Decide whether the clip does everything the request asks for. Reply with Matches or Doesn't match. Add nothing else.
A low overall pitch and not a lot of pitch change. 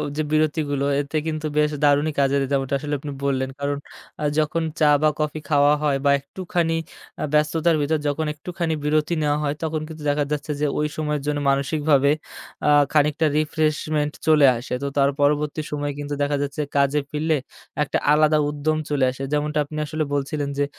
Doesn't match